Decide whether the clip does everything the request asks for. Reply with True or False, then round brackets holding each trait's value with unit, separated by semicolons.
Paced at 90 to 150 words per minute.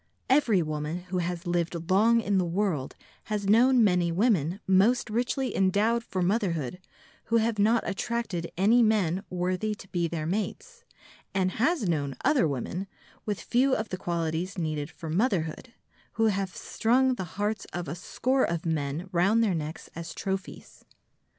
False (160 wpm)